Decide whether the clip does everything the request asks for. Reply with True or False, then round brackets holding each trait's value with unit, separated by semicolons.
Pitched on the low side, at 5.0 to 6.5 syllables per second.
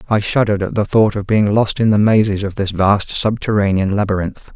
True (100 Hz; 5.5 syllables/s)